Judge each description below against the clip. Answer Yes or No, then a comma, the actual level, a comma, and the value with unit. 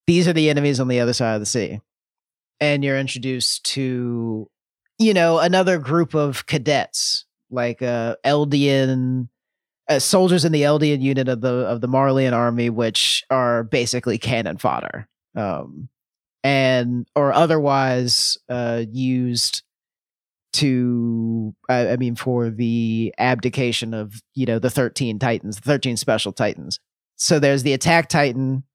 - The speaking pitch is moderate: No, low, 125 Hz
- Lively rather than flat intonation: No, average, 2.9 semitones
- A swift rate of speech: No, average, 145 wpm